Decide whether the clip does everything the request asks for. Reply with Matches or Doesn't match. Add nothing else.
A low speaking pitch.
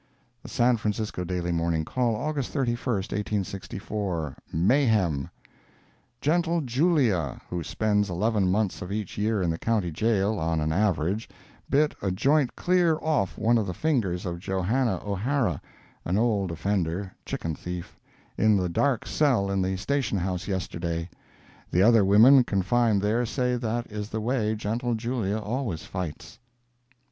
Matches